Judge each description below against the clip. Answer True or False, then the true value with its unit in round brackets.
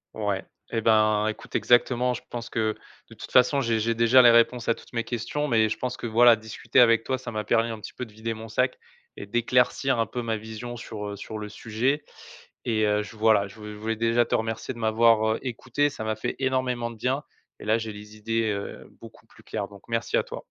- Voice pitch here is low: True (115 Hz)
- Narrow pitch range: True (1.9 semitones)